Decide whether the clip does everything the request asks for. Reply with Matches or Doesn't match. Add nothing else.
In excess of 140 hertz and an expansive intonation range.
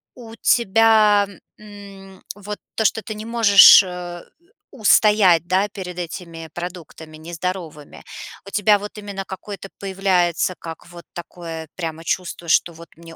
Doesn't match